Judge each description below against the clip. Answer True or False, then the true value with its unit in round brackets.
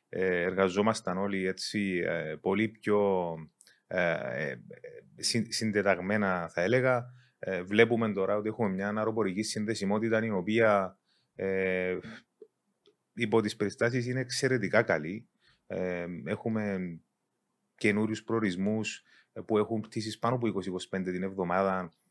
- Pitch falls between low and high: False (105 Hz)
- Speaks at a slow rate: True (90 wpm)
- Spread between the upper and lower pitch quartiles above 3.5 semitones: False (3.1 semitones)